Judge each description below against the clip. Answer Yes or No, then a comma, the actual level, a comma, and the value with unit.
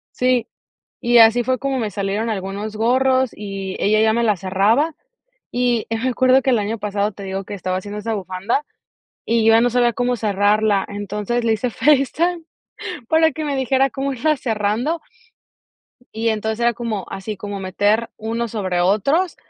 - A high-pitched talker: Yes, high, 225 Hz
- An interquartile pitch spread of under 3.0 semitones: No, average, 3.6 semitones